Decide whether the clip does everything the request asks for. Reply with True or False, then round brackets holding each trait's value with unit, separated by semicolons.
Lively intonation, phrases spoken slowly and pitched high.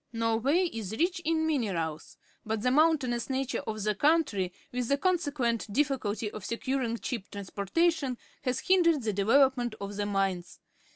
False (5.7 semitones; 160 wpm; 240 Hz)